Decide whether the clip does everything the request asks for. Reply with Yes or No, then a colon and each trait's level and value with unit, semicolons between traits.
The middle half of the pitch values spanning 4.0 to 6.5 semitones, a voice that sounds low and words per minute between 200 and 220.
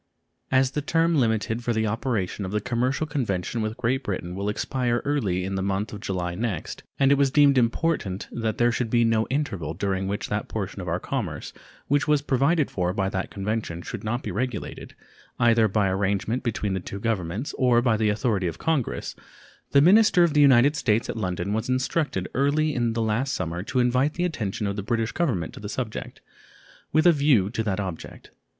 Yes: average, 5.1 semitones; low, 115 Hz; fast, 205 wpm